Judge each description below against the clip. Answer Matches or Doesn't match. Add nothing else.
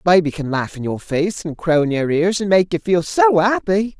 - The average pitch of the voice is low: Doesn't match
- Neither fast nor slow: Doesn't match